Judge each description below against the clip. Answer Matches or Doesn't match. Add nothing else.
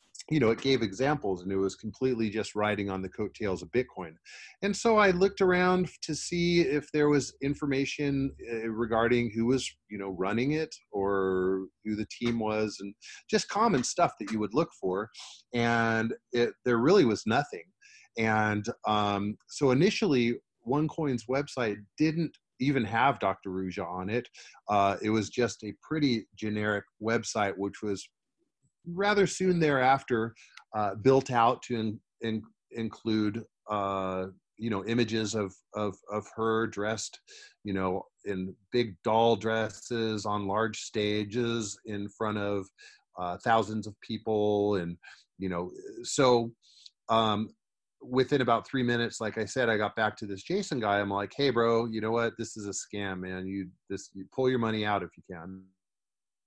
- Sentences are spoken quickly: Doesn't match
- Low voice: Matches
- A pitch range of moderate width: Matches